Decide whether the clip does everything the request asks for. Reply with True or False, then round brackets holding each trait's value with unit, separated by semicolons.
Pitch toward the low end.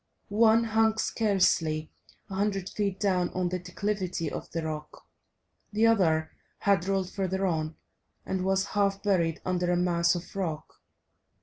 False (185 Hz)